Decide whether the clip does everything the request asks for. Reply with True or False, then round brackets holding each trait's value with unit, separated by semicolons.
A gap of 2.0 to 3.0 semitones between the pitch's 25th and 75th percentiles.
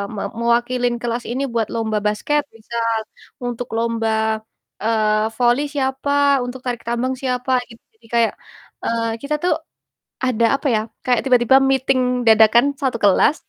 True (2.4 semitones)